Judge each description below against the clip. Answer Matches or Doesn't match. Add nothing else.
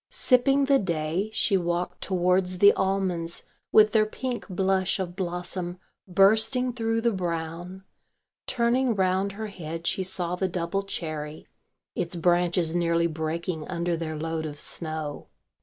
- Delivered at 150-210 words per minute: Doesn't match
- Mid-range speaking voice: Matches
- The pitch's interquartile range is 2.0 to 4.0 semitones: Matches